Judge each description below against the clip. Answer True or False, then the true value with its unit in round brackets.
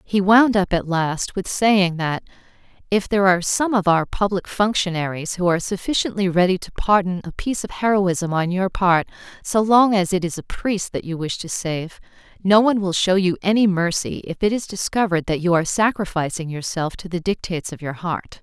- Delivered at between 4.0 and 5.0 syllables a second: False (5.4 syllables/s)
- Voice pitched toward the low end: False (185 Hz)